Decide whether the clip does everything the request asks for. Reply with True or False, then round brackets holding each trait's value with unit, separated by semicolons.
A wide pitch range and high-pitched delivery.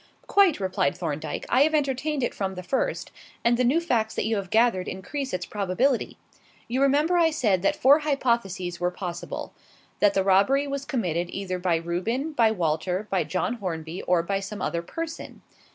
True (7.0 semitones; 205 Hz)